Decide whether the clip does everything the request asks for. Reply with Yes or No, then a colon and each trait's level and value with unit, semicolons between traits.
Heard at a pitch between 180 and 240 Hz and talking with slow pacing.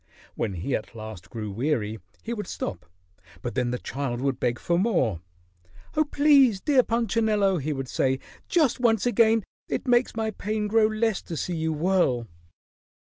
No: medium, 185 Hz; average, 170 wpm